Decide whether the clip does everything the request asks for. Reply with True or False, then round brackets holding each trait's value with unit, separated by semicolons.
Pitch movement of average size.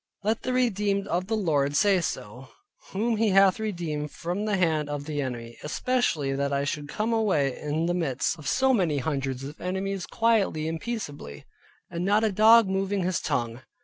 False (6.3 semitones)